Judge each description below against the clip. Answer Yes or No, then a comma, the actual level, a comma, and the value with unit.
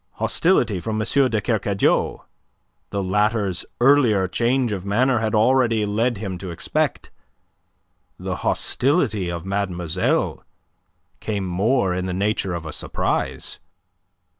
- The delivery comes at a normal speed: No, slow, 120 wpm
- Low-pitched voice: Yes, low, 105 Hz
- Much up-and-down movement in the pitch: No, average, 3.7 semitones